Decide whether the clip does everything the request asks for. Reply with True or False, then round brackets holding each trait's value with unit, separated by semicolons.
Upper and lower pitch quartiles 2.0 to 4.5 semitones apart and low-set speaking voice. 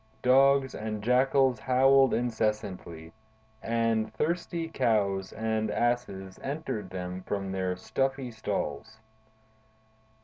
False (5.0 semitones; 110 Hz)